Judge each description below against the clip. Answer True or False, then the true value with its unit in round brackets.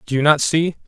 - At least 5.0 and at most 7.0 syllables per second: True (6.0 syllables/s)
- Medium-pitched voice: True (150 Hz)